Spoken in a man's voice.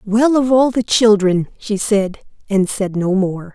No: female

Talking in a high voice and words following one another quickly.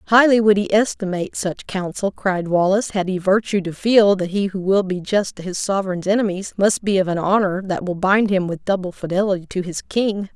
Yes: high, 195 Hz; fast, 220 wpm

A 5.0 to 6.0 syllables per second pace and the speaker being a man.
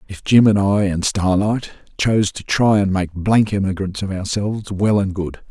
No: 4.8 syllables/s; male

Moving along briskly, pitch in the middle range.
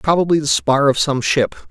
Yes: fast, 210 wpm; medium, 145 Hz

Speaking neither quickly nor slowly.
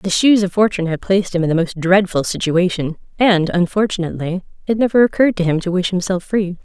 No: fast, 210 wpm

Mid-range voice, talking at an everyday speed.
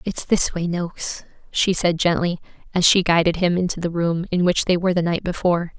No: medium, 175 Hz; fast, 220 wpm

